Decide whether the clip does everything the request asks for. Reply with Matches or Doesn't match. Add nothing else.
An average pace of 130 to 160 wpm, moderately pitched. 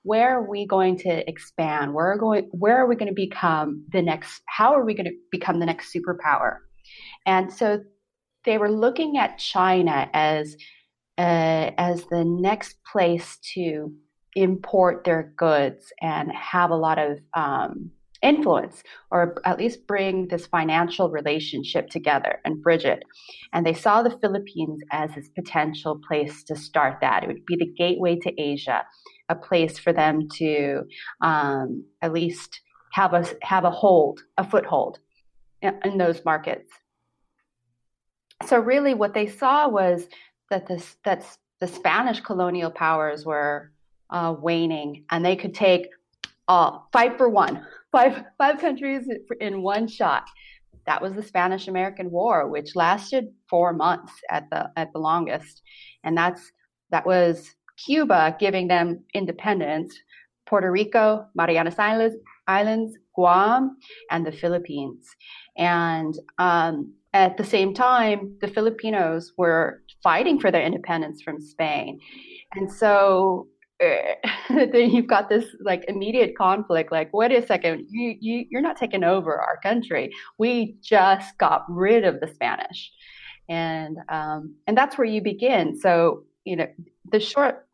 Matches